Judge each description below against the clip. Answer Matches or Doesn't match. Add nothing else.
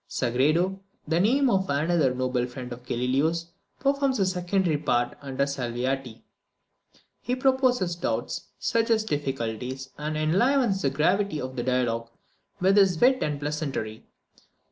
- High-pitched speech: Doesn't match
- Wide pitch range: Matches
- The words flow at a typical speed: Doesn't match